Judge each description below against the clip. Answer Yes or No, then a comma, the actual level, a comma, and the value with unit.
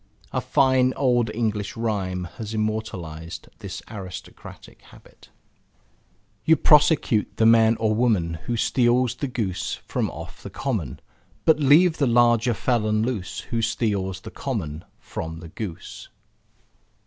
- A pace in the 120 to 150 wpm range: Yes, slow, 135 wpm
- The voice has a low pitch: Yes, low, 110 Hz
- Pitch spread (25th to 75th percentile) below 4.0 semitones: No, average, 4.3 semitones